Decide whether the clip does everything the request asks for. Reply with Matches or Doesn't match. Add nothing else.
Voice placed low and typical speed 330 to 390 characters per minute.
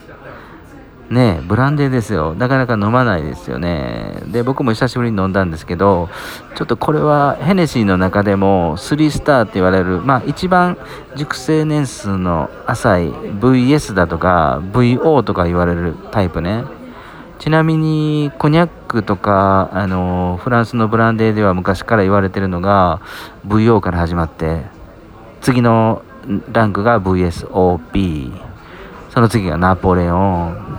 Doesn't match